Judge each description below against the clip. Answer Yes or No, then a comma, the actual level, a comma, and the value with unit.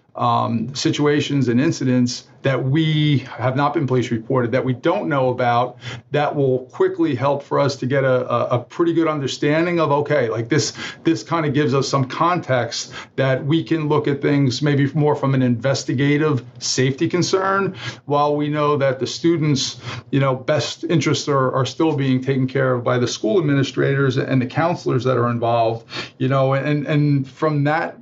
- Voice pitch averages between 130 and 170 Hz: Yes, low, 135 Hz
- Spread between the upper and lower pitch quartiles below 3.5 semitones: Yes, average, 2.8 semitones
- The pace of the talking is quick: No, average, 185 wpm